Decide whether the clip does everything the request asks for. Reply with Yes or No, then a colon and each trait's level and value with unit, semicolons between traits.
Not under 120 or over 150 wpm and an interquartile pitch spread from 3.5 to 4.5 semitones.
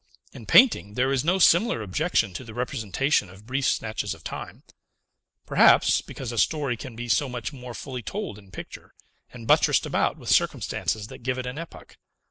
No: average, 185 wpm; average, 4.2 semitones